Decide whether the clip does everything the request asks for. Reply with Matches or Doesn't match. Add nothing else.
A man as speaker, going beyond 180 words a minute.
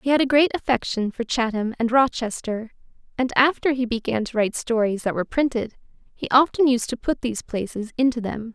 Doesn't match